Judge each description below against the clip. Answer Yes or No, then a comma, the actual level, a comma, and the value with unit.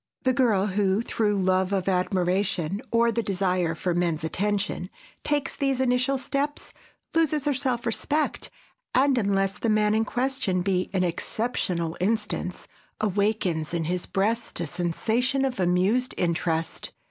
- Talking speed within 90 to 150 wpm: Yes, average, 140 wpm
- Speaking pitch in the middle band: No, high, 200 Hz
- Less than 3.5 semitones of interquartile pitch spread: No, average, 5.3 semitones